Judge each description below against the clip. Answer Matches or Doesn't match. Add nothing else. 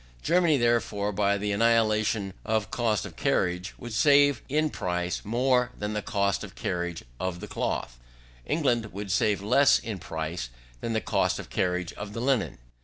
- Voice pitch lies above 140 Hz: Doesn't match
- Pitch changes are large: Doesn't match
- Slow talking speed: Doesn't match